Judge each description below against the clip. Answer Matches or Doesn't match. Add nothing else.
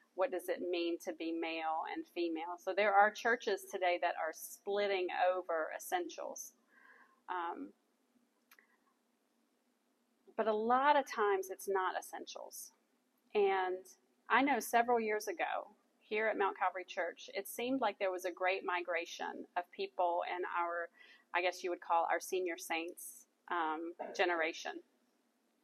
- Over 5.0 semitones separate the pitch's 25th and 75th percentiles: Matches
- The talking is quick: Doesn't match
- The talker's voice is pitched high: Matches